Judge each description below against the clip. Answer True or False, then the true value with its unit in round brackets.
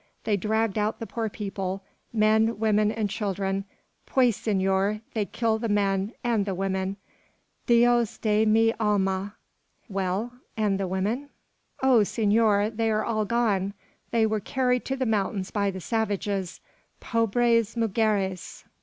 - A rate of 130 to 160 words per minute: True (140 wpm)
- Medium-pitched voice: False (215 Hz)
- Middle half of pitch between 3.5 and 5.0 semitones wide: False (2.5 semitones)